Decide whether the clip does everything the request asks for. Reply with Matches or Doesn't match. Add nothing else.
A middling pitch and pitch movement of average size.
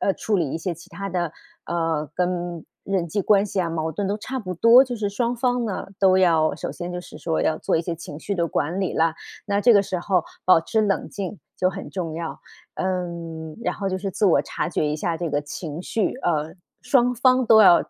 Matches